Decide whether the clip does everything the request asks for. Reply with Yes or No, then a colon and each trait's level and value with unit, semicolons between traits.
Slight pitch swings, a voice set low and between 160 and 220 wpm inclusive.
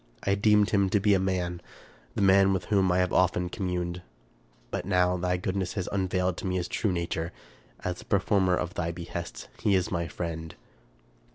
Yes: narrow, 1.7 semitones; very low, 90 Hz; average, 195 wpm